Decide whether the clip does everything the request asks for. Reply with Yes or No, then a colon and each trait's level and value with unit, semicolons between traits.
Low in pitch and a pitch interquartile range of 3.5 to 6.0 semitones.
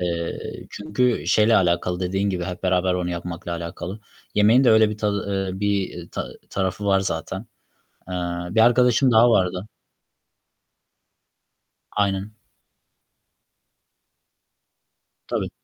No: very low, 95 Hz; average, 2.9 semitones